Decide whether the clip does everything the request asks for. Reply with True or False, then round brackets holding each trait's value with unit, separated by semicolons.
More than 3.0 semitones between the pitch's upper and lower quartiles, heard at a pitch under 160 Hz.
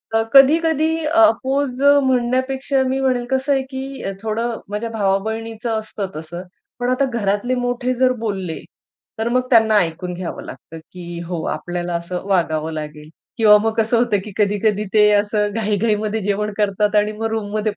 False (4.1 semitones; 220 Hz)